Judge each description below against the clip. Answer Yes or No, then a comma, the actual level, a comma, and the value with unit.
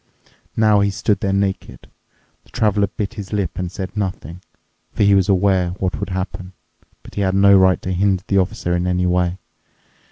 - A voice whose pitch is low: Yes, very low, 95 Hz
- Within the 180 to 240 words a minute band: Yes, average, 190 wpm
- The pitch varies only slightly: Yes, narrow, 1.8 semitones